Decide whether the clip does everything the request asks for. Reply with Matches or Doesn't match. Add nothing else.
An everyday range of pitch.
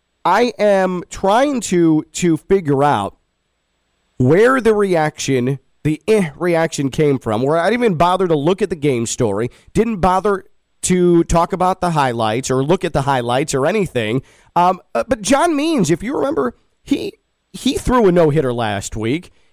Doesn't match